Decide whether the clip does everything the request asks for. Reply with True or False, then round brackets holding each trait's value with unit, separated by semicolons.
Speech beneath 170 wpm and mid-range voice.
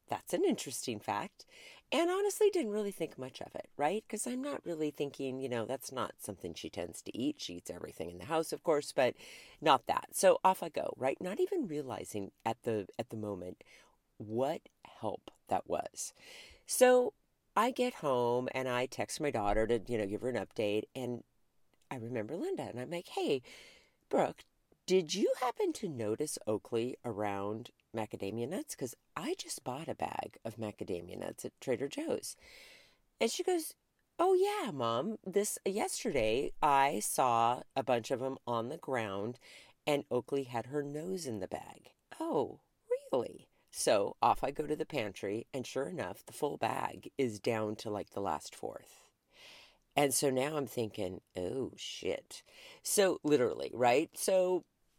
False (175 wpm; 145 Hz)